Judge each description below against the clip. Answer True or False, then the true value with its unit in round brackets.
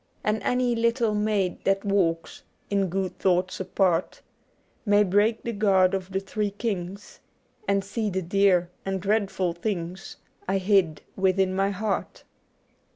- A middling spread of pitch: False (2.0 semitones)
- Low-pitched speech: False (195 Hz)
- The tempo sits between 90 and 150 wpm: True (145 wpm)